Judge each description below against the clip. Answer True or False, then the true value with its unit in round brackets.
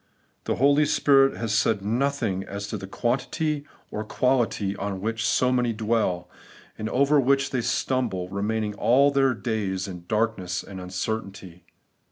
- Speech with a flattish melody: False (4.9 semitones)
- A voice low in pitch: True (110 Hz)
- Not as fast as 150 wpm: False (155 wpm)